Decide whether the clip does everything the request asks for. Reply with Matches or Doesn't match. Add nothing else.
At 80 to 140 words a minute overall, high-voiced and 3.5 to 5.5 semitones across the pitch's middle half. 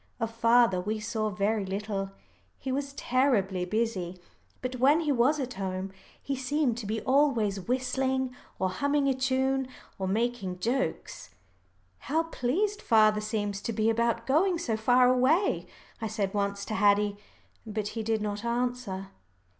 Doesn't match